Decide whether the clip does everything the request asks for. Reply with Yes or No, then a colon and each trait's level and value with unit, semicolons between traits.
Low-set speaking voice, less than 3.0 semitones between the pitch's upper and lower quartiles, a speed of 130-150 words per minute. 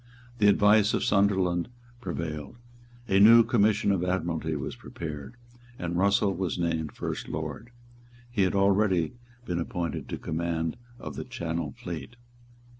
No: very low, 90 Hz; average, 3.7 semitones; average, 140 wpm